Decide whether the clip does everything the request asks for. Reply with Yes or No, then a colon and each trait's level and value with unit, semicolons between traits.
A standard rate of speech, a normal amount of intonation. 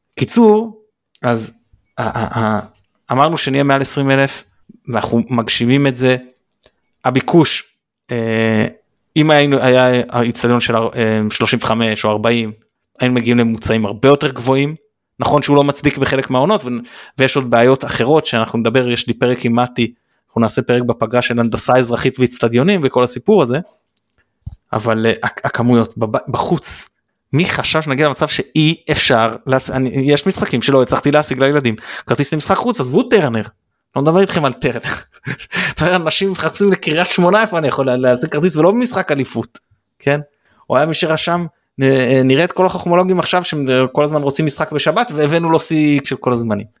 No: fast, 160 wpm; average, 4.6 semitones